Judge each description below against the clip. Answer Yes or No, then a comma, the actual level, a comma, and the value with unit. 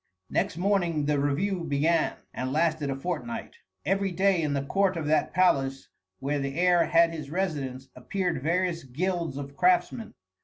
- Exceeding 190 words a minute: No, average, 160 wpm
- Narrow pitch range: No, average, 4.4 semitones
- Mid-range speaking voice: Yes, medium, 165 Hz